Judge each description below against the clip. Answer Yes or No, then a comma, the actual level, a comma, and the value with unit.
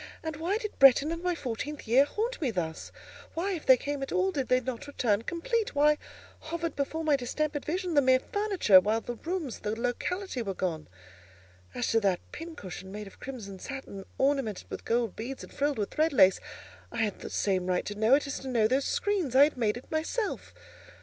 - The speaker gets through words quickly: Yes, fast, 210 wpm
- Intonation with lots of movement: Yes, wide, 6.3 semitones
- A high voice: Yes, very high, 270 Hz